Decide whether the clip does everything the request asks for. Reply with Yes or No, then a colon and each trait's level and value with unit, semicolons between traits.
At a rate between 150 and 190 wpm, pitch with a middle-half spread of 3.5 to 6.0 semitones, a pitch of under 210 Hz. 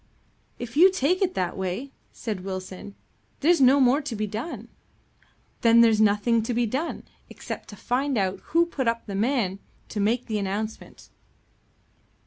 No: average, 155 wpm; average, 4.8 semitones; high, 230 Hz